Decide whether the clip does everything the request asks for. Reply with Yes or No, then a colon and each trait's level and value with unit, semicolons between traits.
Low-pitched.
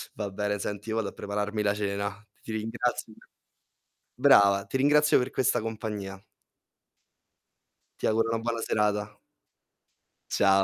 Yes: low, 105 Hz